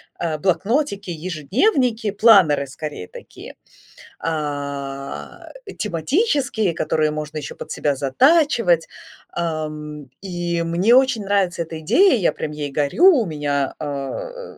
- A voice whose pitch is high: No, medium, 170 Hz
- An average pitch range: No, wide, 6.6 semitones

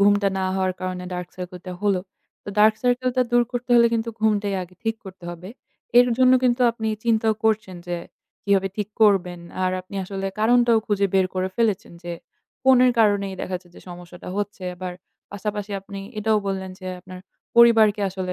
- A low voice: No, high, 200 Hz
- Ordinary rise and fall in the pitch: Yes, average, 3.2 semitones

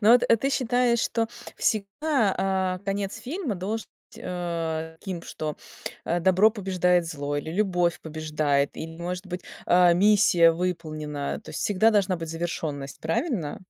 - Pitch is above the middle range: No, medium, 180 Hz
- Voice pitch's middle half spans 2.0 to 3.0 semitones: No, average, 4.3 semitones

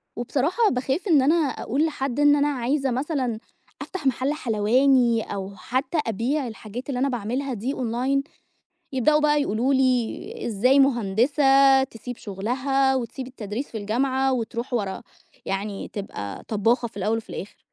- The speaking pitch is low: No, very high, 255 Hz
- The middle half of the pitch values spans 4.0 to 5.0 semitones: No, average, 3.4 semitones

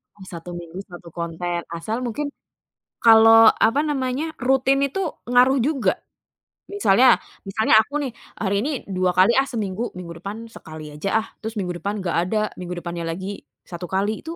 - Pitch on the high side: Yes, high, 210 Hz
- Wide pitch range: Yes, wide, 5.9 semitones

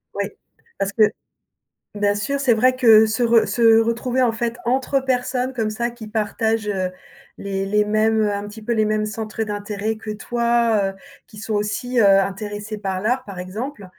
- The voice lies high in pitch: Yes, high, 220 Hz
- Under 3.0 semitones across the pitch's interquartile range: Yes, narrow, 2.4 semitones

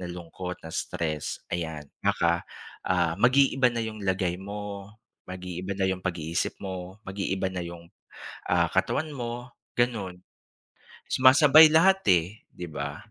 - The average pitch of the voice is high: No, very low, 95 Hz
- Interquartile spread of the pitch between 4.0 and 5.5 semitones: Yes, average, 5.0 semitones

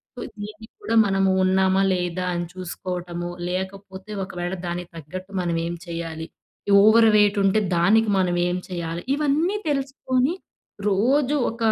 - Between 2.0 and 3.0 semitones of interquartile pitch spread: No, average, 4.0 semitones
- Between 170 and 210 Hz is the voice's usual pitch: Yes, high, 190 Hz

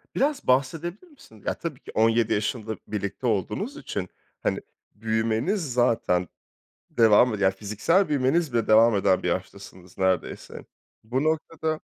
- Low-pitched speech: Yes, low, 115 Hz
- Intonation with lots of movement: Yes, wide, 6.9 semitones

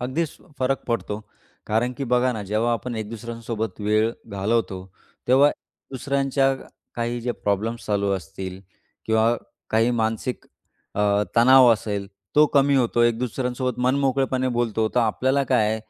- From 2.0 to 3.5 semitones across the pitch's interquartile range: Yes, average, 2.9 semitones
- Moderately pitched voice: No, low, 115 Hz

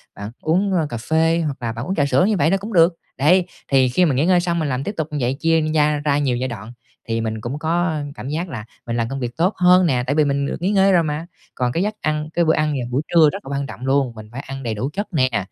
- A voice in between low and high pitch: Yes, medium, 150 Hz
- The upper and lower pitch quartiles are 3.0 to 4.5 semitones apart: No, average, 5.1 semitones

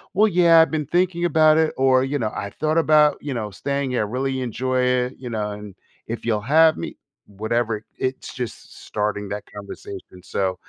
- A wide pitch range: Yes, wide, 6.3 semitones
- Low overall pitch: Yes, low, 130 Hz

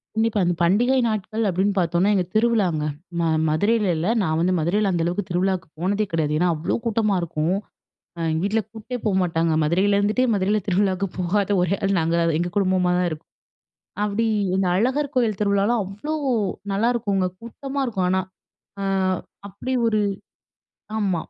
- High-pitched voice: Yes, high, 195 Hz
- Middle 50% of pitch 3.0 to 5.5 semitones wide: Yes, average, 3.4 semitones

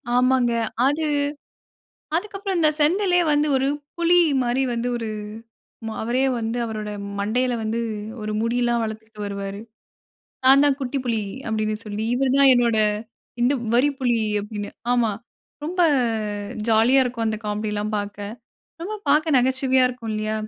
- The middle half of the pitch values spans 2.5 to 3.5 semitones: No, average, 3.9 semitones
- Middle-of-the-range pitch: No, high, 240 Hz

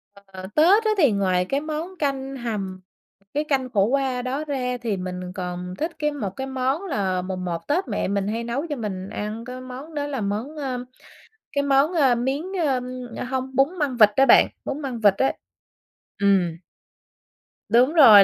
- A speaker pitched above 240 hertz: Yes, very high, 255 Hz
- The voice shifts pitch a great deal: Yes, wide, 5.9 semitones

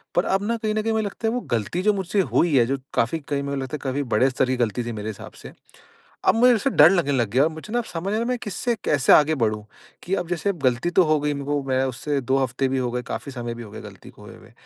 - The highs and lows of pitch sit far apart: Yes, wide, 7.3 semitones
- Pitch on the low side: No, medium, 145 Hz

